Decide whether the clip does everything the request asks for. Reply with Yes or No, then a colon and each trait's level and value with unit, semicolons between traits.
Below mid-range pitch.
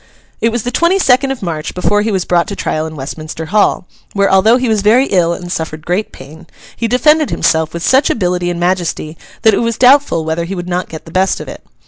No: high, 190 Hz